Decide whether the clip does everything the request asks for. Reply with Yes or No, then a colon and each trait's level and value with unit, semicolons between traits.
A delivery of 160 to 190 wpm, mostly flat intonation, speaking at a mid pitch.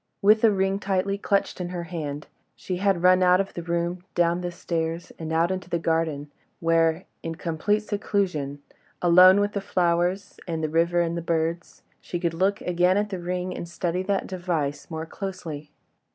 Yes: average, 185 wpm; narrow, 2.2 semitones; medium, 175 Hz